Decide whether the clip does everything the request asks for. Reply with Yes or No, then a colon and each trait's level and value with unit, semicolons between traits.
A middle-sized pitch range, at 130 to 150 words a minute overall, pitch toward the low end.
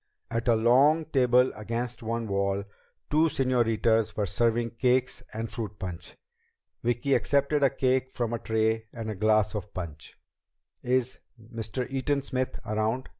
Yes: average, 3.0 semitones; average, 145 wpm; low, 115 Hz